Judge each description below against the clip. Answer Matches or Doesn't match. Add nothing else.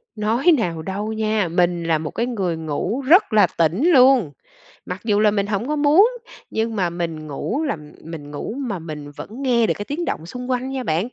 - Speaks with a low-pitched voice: Doesn't match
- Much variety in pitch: Matches